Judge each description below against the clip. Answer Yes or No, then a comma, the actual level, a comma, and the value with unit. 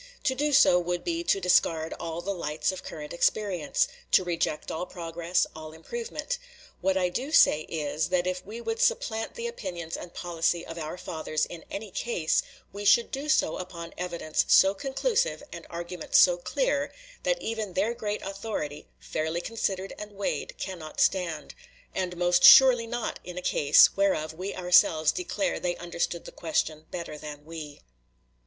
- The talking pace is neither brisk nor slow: Yes, average, 170 wpm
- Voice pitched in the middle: Yes, medium, 180 Hz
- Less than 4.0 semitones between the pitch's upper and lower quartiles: No, average, 4.5 semitones